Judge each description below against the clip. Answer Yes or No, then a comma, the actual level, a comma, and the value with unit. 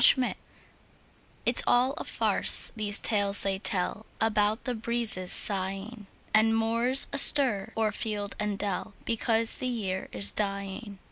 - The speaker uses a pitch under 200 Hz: No, high, 215 Hz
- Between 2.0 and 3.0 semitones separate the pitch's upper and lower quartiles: Yes, narrow, 2.6 semitones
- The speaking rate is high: No, average, 140 wpm